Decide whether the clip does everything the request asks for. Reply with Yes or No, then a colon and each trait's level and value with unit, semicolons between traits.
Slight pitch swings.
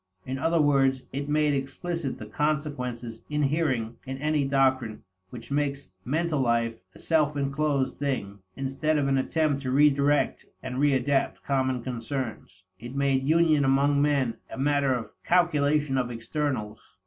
Yes: narrow, 2.3 semitones